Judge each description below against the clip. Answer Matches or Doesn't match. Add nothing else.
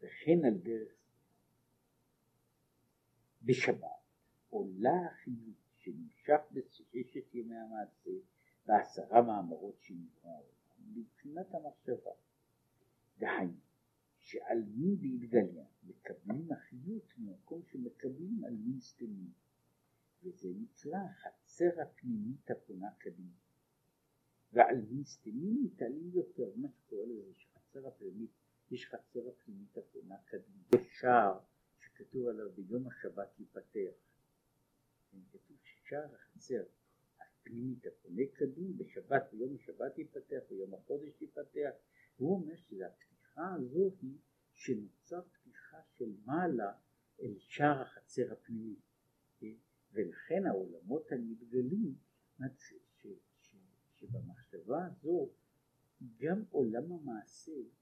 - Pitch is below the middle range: Doesn't match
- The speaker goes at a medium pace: Doesn't match